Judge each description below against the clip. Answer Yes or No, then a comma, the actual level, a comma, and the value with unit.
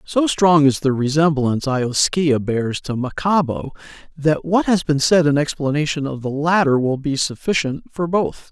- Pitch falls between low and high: Yes, medium, 150 Hz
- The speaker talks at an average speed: Yes, average, 170 wpm